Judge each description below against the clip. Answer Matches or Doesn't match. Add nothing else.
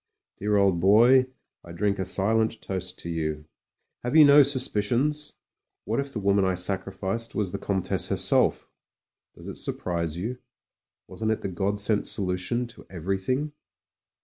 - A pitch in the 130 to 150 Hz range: Doesn't match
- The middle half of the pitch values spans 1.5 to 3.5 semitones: Doesn't match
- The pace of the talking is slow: Doesn't match